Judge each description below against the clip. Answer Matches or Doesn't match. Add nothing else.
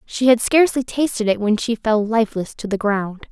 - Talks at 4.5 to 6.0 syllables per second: Matches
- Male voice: Doesn't match